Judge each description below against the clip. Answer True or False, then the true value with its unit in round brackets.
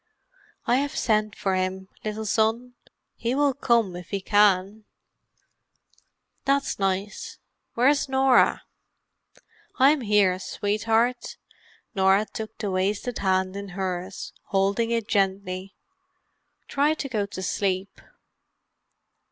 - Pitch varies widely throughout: False (3.7 semitones)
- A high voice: True (210 Hz)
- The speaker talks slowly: True (110 wpm)